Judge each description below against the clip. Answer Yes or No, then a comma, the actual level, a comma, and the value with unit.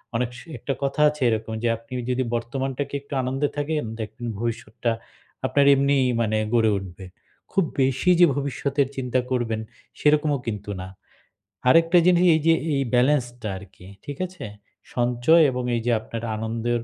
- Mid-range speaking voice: No, low, 125 Hz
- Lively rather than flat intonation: No, average, 3.7 semitones